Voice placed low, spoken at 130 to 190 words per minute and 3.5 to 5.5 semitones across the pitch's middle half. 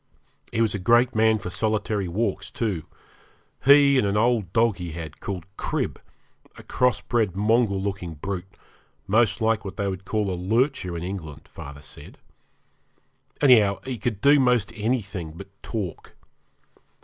Yes: low, 105 Hz; average, 150 wpm; average, 4.0 semitones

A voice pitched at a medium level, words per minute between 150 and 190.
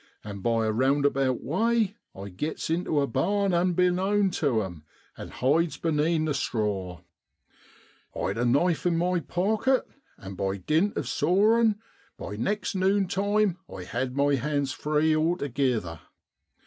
No: medium, 150 Hz; slow, 135 wpm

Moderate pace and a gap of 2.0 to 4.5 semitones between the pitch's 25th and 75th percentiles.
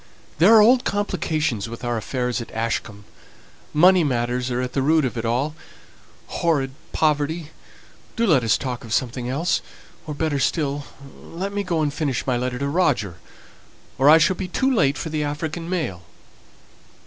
No: average, 170 wpm; average, 5.0 semitones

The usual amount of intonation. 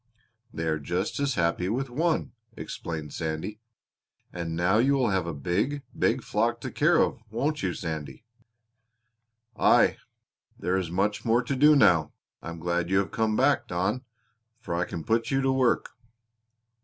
No: wide, 7.1 semitones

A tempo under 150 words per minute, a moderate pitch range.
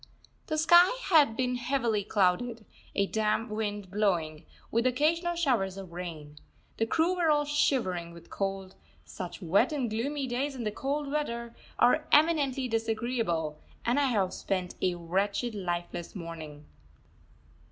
No: average, 140 wpm; wide, 6.7 semitones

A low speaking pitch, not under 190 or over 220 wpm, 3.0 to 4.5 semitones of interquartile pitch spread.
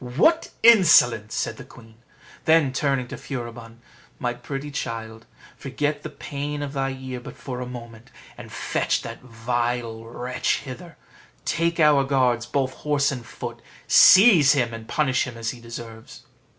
No: low, 130 Hz; average, 155 wpm; average, 3.6 semitones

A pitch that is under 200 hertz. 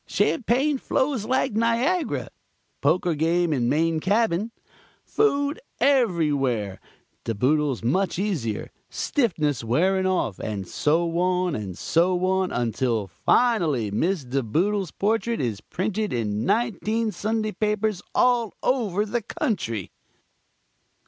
Yes: medium, 185 Hz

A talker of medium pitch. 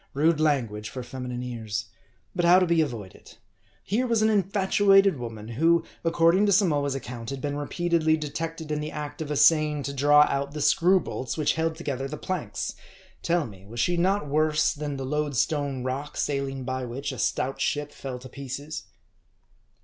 Yes: medium, 145 Hz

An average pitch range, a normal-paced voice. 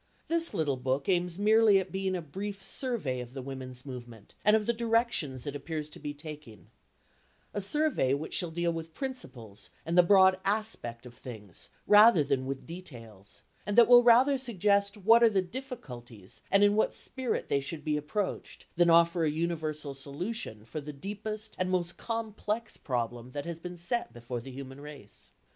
No: wide, 7.5 semitones; average, 180 wpm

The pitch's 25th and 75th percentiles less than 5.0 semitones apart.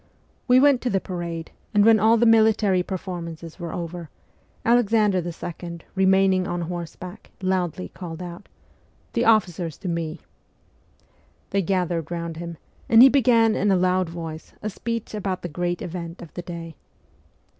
Yes: average, 3.6 semitones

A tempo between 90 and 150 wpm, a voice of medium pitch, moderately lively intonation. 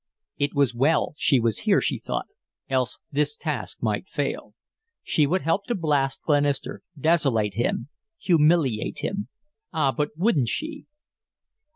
Yes: average, 140 wpm; medium, 145 Hz; average, 3.7 semitones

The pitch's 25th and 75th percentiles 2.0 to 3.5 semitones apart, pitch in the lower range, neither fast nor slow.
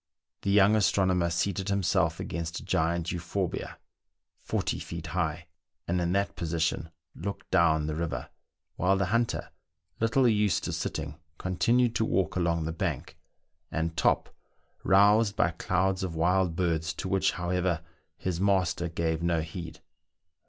Yes: average, 2.9 semitones; very low, 90 Hz; average, 145 wpm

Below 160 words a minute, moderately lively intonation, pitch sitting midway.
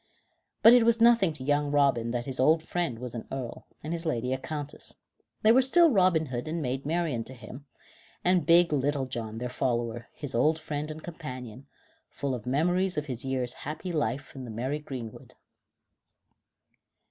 No: average, 185 wpm; average, 4.7 semitones; medium, 145 Hz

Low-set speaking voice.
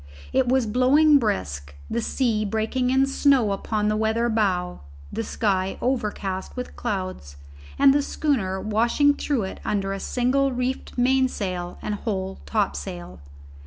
No: high, 220 Hz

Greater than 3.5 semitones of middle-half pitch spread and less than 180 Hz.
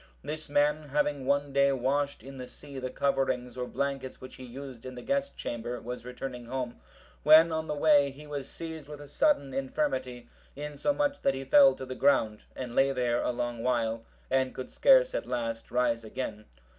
No: average, 2.8 semitones; low, 135 Hz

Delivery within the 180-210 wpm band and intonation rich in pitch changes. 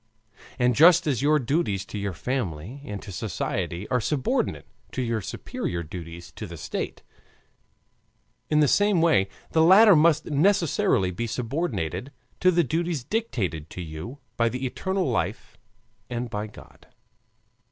No: average, 145 wpm; wide, 8.4 semitones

